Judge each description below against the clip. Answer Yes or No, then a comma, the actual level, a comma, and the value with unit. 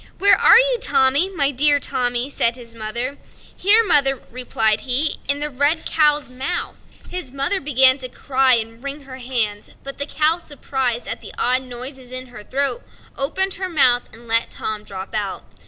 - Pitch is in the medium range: No, very high, 265 Hz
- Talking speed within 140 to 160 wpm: No, average, 180 wpm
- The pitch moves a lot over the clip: No, average, 3.3 semitones